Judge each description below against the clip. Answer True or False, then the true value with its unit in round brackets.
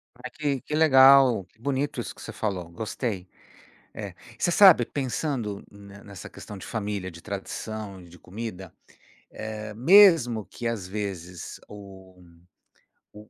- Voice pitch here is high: False (105 Hz)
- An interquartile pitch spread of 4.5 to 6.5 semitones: True (4.9 semitones)